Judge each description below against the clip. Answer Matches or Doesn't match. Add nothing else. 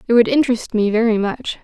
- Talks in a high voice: Matches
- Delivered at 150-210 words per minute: Doesn't match